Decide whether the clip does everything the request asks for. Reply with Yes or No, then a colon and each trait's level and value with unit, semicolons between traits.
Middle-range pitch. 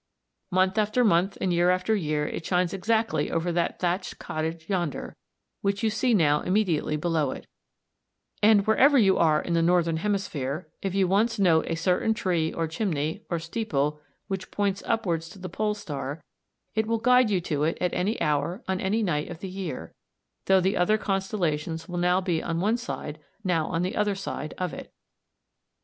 Yes: medium, 180 Hz